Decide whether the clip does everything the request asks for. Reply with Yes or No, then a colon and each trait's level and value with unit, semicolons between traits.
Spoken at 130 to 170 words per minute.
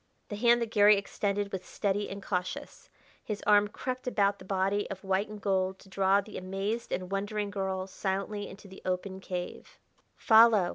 No: average, 180 wpm